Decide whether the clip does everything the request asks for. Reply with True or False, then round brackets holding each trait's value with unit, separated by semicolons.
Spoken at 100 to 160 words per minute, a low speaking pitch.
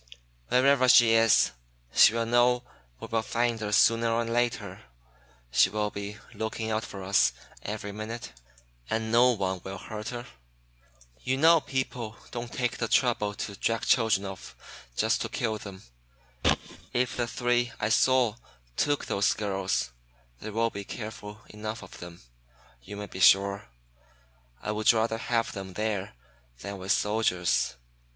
True (150 wpm; 110 Hz)